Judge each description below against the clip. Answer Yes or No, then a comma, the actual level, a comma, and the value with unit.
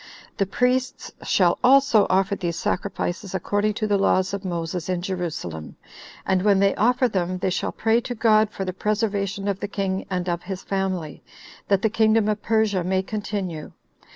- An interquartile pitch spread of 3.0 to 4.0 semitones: No, narrow, 2.6 semitones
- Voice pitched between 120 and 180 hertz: No, high, 195 Hz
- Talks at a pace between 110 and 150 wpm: No, average, 180 wpm